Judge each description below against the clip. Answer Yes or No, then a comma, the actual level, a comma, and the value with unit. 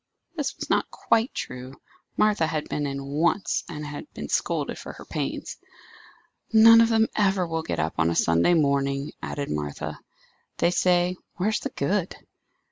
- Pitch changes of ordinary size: No, wide, 6.7 semitones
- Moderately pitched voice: Yes, medium, 165 Hz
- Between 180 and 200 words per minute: No, average, 165 wpm